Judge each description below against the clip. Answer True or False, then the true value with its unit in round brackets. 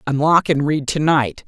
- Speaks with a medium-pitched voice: True (150 Hz)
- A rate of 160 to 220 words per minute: True (205 wpm)